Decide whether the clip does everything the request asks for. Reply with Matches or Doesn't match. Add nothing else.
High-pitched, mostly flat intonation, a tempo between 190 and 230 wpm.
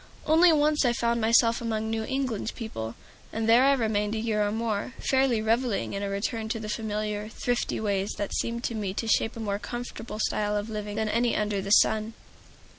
Matches